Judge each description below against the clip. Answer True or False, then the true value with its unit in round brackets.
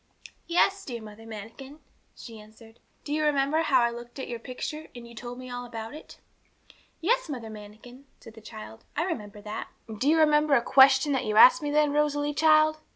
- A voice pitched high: True (255 Hz)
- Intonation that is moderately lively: True (5.0 semitones)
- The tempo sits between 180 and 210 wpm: True (205 wpm)